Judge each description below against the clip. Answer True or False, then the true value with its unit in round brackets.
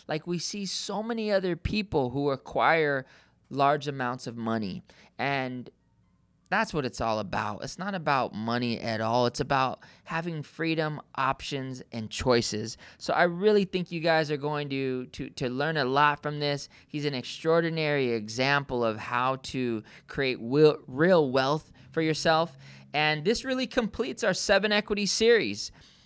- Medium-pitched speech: True (145 Hz)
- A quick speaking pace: False (155 wpm)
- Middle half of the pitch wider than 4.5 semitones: True (4.9 semitones)